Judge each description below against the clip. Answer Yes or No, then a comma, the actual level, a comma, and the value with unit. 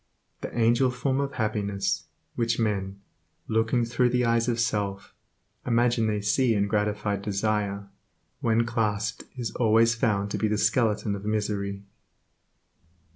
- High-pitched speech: No, low, 110 Hz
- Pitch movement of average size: No, narrow, 2.3 semitones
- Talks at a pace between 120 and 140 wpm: Yes, slow, 135 wpm